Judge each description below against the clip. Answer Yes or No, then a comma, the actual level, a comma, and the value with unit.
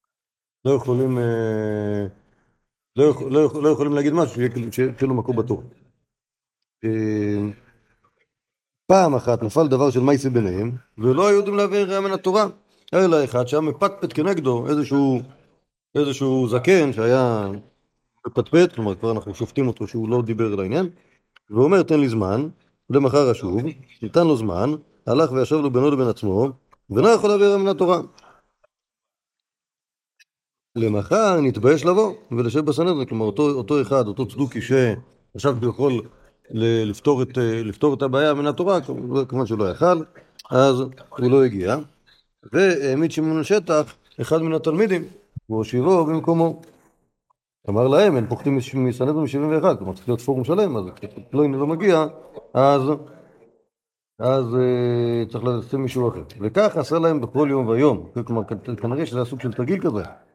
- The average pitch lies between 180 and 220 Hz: No, low, 135 Hz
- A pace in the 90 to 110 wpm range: No, average, 145 wpm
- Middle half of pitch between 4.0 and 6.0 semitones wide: Yes, average, 4.7 semitones